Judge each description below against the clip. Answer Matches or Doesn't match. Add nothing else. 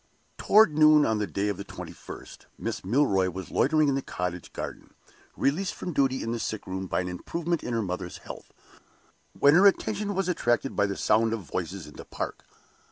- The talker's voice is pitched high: Doesn't match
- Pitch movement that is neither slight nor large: Doesn't match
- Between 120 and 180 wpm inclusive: Doesn't match